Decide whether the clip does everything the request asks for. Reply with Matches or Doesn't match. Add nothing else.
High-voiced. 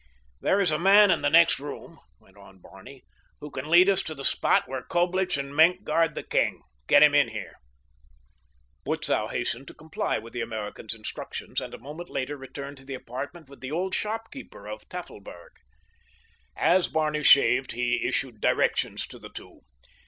Doesn't match